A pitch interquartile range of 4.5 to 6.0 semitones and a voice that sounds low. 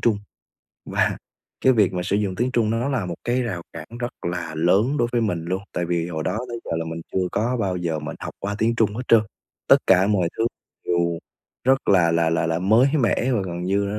Yes: average, 5.0 semitones; very low, 95 Hz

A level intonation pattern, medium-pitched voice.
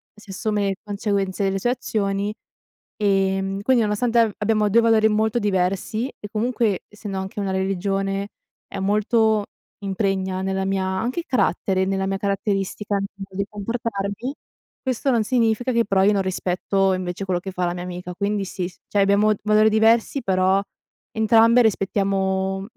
No: narrow, 2.2 semitones; high, 200 Hz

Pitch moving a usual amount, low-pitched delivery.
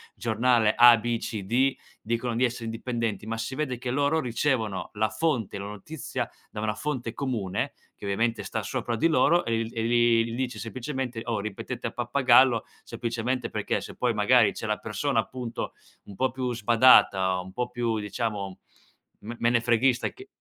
No: narrow, 2.3 semitones; low, 120 Hz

